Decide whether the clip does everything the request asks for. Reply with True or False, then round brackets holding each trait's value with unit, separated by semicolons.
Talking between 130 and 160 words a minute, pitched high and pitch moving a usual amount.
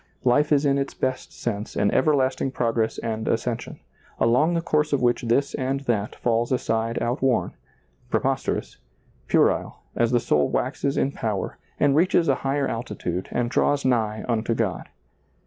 False (155 wpm; 120 Hz; 3.4 semitones)